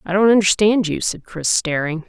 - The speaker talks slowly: No, average, 200 wpm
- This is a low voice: No, medium, 185 Hz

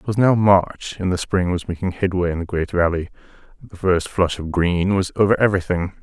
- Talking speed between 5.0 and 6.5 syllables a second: Yes, 5.5 syllables/s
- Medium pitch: No, very low, 90 Hz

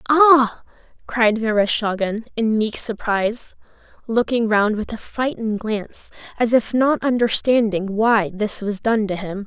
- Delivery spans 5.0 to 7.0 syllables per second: No, 4.3 syllables/s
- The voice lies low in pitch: No, high, 225 Hz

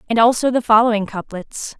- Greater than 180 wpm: No, average, 165 wpm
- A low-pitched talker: No, high, 225 Hz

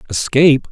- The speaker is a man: Yes, male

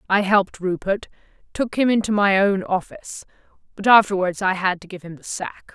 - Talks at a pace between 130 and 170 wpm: No, average, 190 wpm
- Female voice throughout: Yes, female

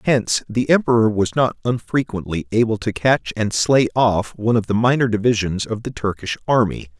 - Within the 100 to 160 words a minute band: No, average, 180 wpm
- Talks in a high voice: No, low, 110 Hz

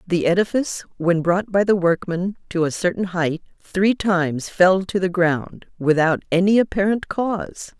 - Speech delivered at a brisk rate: No, average, 160 wpm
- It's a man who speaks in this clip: No, female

